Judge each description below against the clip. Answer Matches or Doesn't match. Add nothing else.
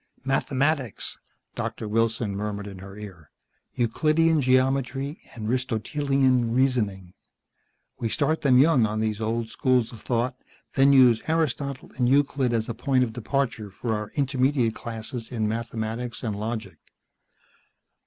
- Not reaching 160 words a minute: Matches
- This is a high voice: Doesn't match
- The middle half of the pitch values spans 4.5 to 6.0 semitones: Doesn't match